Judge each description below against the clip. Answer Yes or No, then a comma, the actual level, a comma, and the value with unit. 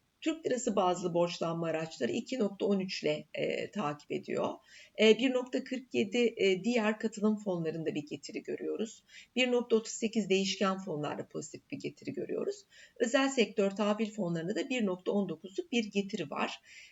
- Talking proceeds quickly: No, average, 125 wpm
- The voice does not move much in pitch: No, average, 4.5 semitones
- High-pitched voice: Yes, high, 215 Hz